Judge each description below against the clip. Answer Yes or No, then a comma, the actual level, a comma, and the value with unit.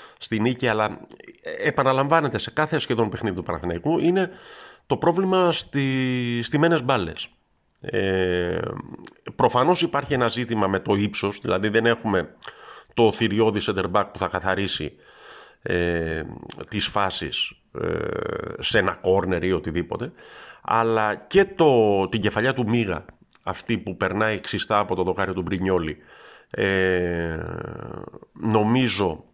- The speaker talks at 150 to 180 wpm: No, average, 125 wpm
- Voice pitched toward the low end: Yes, low, 110 Hz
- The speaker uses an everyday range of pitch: No, wide, 5.9 semitones